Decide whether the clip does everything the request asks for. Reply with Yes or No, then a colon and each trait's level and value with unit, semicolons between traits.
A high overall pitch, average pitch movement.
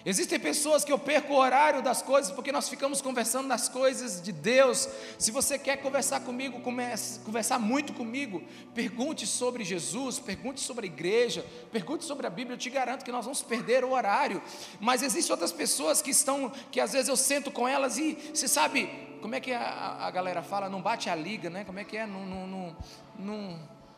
Yes: very high, 255 Hz; average, 3.3 semitones